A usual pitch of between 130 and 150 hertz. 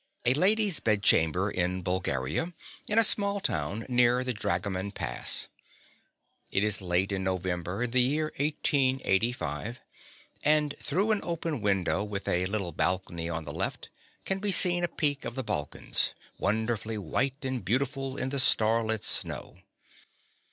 No: low, 115 Hz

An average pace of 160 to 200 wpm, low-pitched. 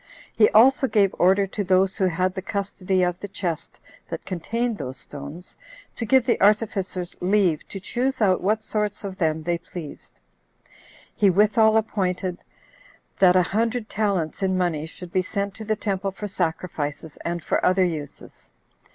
No: average, 165 wpm; high, 190 Hz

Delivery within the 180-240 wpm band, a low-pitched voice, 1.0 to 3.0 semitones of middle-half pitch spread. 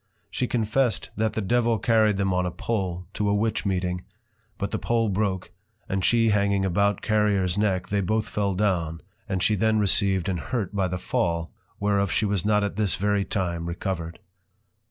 Yes: average, 185 wpm; low, 100 Hz; narrow, 2.6 semitones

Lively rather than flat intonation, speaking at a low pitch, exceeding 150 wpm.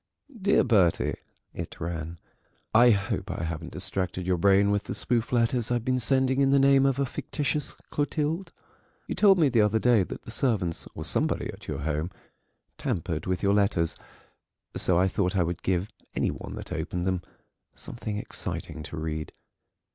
Yes: wide, 6.6 semitones; low, 100 Hz; average, 175 wpm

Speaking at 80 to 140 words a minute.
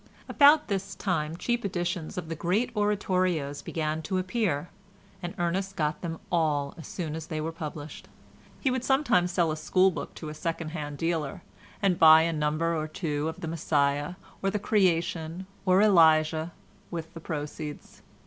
No: average, 170 wpm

